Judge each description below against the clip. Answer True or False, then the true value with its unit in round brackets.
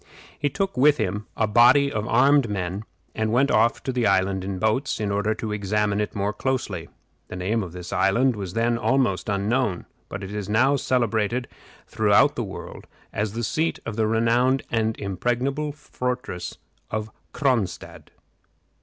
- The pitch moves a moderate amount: True (3.9 semitones)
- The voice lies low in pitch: True (110 Hz)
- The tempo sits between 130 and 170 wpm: True (165 wpm)